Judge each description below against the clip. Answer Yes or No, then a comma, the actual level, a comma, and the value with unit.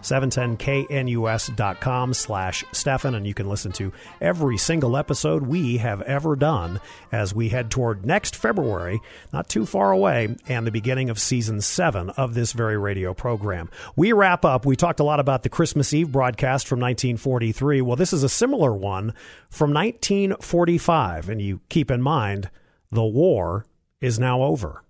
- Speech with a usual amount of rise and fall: Yes, average, 4.7 semitones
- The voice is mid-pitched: No, low, 125 Hz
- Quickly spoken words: No, average, 165 wpm